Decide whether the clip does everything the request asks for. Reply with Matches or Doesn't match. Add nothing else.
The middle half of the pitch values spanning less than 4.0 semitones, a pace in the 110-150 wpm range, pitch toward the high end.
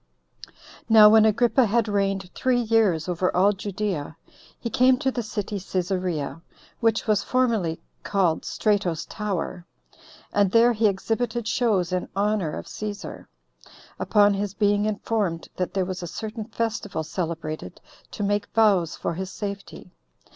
Matches